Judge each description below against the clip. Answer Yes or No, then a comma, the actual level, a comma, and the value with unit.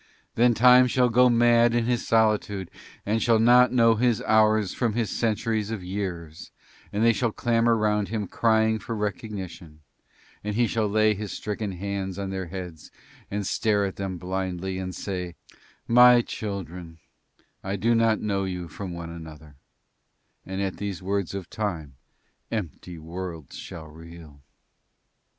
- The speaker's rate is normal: Yes, average, 155 wpm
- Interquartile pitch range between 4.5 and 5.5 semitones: No, average, 3.8 semitones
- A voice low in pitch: Yes, low, 100 Hz